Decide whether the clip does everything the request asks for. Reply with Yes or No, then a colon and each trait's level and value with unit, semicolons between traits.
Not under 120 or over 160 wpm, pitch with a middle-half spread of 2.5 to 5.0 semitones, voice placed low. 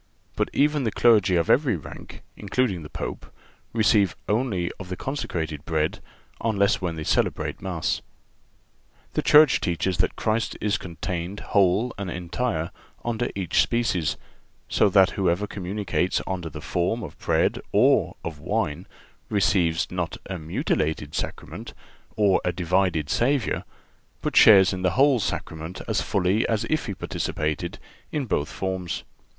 Yes: average, 145 wpm; average, 4.1 semitones; very low, 95 Hz